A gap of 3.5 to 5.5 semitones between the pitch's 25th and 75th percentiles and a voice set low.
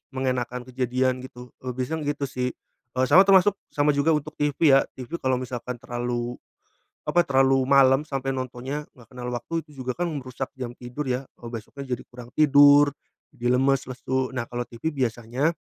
No: narrow, 2.5 semitones; low, 130 Hz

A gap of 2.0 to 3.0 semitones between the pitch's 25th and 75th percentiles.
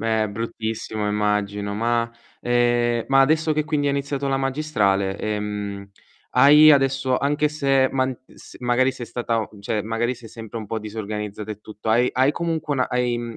No: average, 4.1 semitones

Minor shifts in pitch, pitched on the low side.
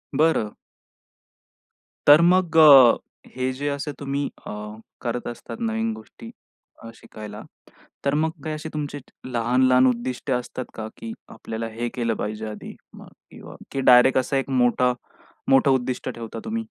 No: average, 3.6 semitones; low, 130 Hz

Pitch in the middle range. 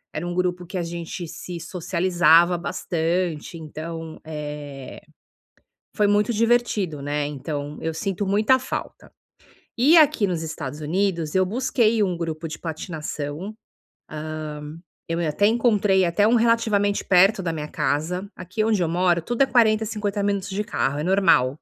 Yes: medium, 180 Hz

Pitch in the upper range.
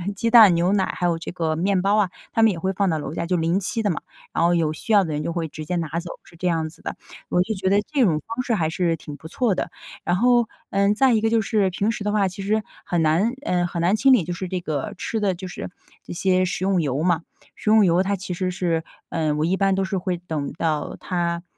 No: medium, 180 Hz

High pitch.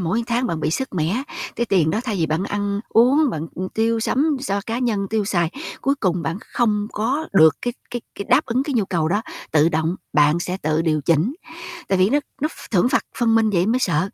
Yes: high, 200 Hz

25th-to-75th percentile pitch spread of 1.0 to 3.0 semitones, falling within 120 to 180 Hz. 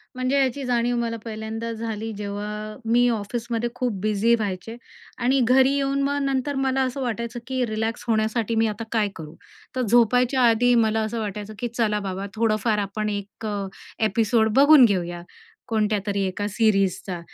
No: average, 2.7 semitones; high, 225 Hz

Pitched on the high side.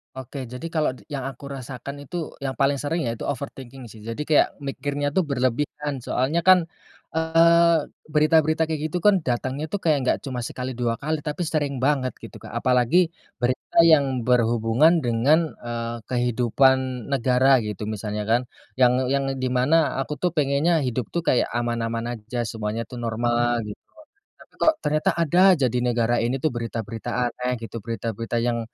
No: low, 130 Hz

